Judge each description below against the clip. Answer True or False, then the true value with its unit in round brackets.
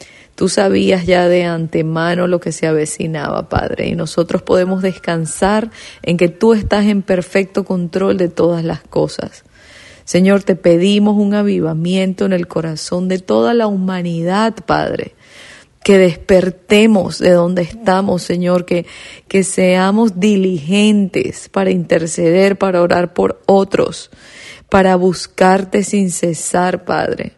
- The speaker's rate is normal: False (130 wpm)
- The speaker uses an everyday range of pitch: False (2.1 semitones)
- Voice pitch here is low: False (185 Hz)